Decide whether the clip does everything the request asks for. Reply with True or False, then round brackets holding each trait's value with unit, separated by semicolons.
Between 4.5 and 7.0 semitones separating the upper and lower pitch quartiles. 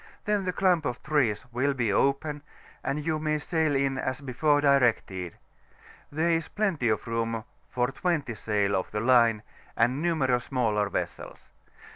True (5.0 semitones)